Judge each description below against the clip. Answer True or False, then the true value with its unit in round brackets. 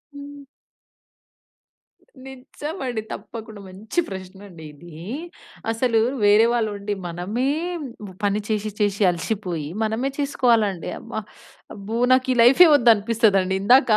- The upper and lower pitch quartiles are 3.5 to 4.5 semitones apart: True (3.9 semitones)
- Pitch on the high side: True (220 Hz)